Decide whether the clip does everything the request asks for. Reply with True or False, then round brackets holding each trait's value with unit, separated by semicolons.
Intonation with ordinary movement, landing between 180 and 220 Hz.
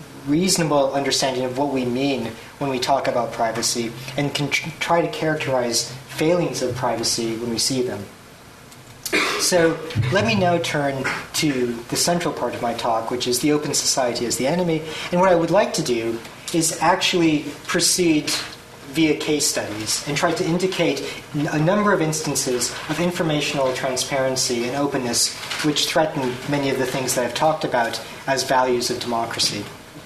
False (4.4 semitones; 140 Hz)